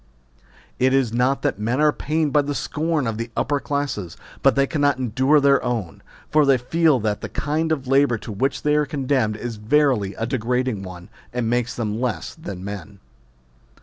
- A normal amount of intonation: Yes, average, 4.4 semitones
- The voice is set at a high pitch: No, low, 130 Hz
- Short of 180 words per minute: No, average, 190 wpm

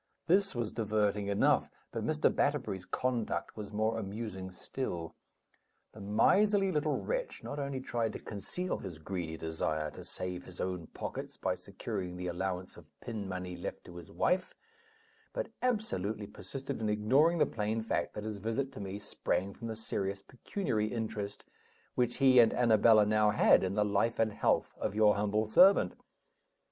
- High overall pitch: No, low, 105 Hz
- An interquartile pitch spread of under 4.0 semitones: No, average, 4.3 semitones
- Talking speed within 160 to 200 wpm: Yes, average, 165 wpm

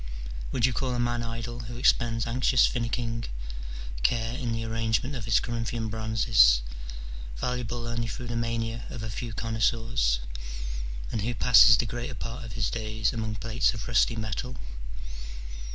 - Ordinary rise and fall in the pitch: No, narrow, 1.3 semitones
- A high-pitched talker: No, low, 115 Hz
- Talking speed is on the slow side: No, average, 155 wpm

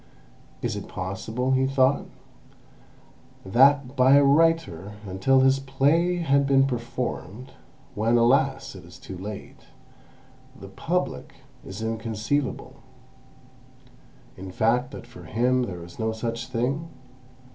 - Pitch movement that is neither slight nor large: Yes, average, 3.4 semitones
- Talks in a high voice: No, low, 125 Hz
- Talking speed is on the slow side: Yes, slow, 115 wpm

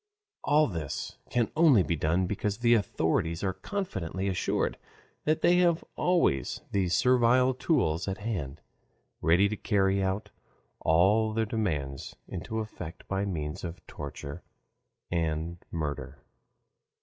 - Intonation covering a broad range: Yes, wide, 5.7 semitones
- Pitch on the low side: Yes, very low, 95 Hz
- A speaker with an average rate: No, slow, 125 wpm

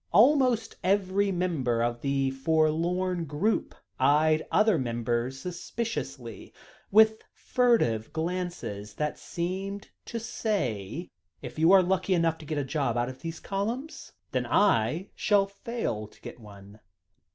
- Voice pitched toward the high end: No, medium, 165 Hz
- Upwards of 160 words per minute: No, slow, 135 wpm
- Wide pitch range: Yes, wide, 7.2 semitones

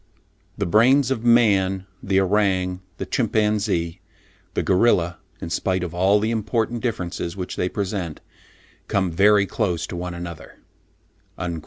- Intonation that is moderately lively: Yes, average, 3.4 semitones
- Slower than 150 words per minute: Yes, average, 140 wpm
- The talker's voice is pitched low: Yes, very low, 95 Hz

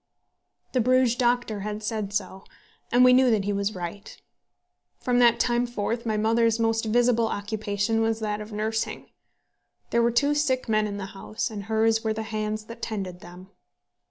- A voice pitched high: Yes, high, 220 Hz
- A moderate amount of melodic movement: No, narrow, 2.2 semitones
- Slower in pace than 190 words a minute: Yes, average, 180 wpm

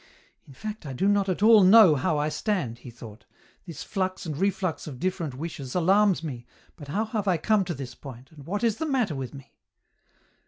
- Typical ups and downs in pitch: No, wide, 6.4 semitones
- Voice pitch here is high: No, medium, 170 Hz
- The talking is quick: Yes, fast, 225 wpm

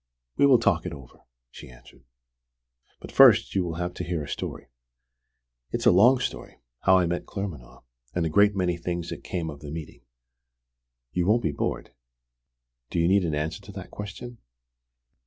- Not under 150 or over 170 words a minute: No, average, 180 wpm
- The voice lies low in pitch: Yes, very low, 90 Hz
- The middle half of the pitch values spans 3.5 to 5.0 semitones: Yes, average, 3.8 semitones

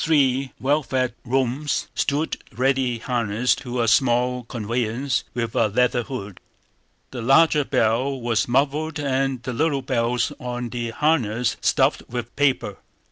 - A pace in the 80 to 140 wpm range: Yes, slow, 135 wpm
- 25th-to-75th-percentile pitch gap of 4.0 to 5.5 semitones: No, narrow, 2.5 semitones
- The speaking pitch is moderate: No, low, 125 Hz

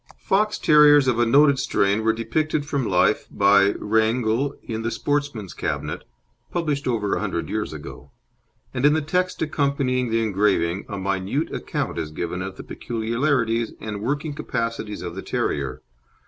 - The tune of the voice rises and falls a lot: Yes, wide, 6.0 semitones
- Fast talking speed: No, average, 160 wpm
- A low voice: Yes, low, 115 Hz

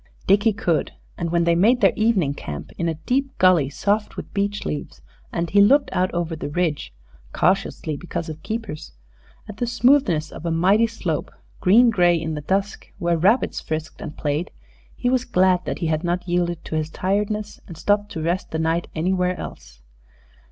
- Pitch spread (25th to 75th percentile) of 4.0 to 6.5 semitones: Yes, average, 4.3 semitones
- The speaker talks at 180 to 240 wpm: Yes, average, 185 wpm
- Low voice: No, medium, 180 Hz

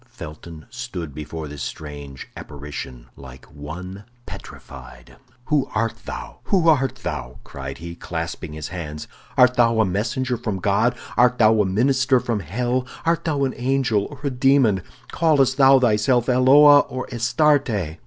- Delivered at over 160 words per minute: No, average, 150 wpm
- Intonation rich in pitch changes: Yes, wide, 8.1 semitones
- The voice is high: No, low, 115 Hz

